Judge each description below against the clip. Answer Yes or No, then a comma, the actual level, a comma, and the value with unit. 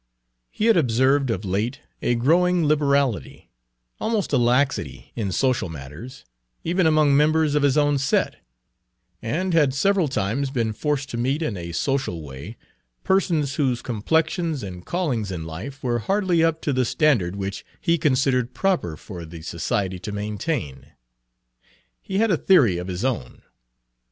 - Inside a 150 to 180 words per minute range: Yes, average, 155 wpm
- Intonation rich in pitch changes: Yes, wide, 7.2 semitones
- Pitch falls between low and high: No, low, 130 Hz